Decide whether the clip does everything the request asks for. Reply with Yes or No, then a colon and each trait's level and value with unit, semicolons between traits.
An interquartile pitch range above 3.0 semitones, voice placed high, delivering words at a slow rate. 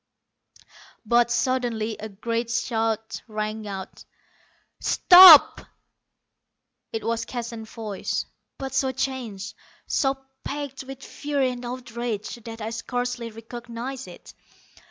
No: narrow, 2.6 semitones; high, 235 Hz; slow, 105 wpm